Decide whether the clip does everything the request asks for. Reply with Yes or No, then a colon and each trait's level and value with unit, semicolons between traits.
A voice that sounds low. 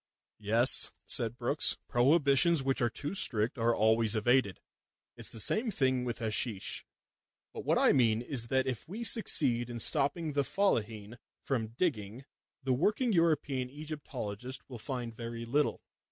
Yes: low, 125 Hz